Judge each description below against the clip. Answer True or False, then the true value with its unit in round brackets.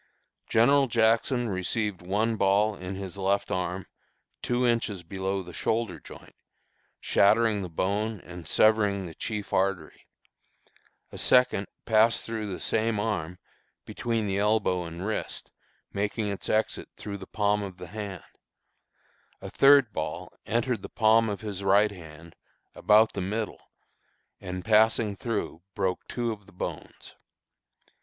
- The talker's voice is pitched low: True (105 Hz)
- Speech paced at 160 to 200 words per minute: False (140 wpm)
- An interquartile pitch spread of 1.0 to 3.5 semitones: True (2.9 semitones)